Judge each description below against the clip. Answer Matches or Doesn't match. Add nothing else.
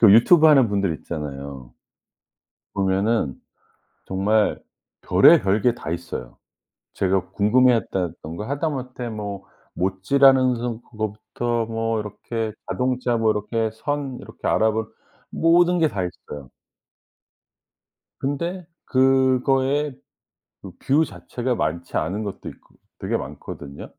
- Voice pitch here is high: Doesn't match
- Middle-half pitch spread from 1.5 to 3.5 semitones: Doesn't match